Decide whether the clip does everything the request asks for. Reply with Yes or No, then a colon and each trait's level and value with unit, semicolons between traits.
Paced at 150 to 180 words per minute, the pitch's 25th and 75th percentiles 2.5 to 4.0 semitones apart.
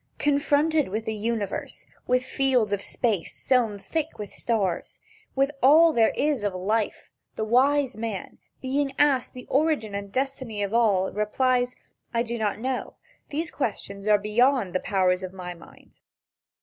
No: average, 155 wpm; average, 4.8 semitones